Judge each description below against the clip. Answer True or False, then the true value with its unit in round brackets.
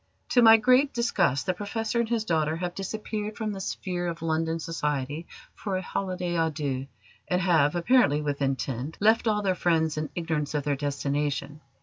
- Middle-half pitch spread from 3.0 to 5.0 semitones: False (5.6 semitones)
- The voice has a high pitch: False (170 Hz)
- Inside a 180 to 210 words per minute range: True (185 wpm)